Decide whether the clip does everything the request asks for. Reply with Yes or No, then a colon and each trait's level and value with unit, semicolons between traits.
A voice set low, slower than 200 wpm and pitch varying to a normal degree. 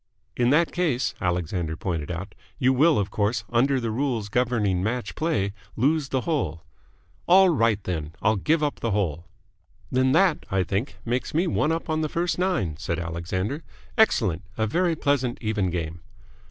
No: low, 115 Hz; average, 170 wpm; wide, 8.3 semitones